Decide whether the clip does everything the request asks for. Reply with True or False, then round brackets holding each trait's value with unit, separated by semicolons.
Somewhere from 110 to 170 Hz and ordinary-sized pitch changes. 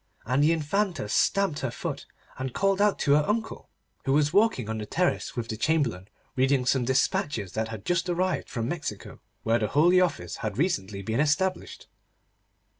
False (140 Hz; 7.8 semitones)